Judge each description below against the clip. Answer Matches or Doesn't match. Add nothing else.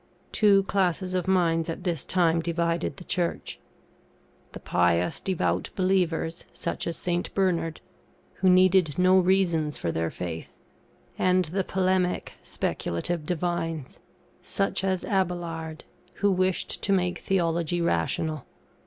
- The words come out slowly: Matches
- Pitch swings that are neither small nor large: Doesn't match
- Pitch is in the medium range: Matches